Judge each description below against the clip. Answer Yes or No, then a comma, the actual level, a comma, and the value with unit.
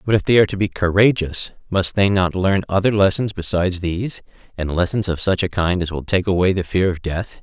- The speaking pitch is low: Yes, very low, 95 Hz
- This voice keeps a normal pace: No, fast, 235 wpm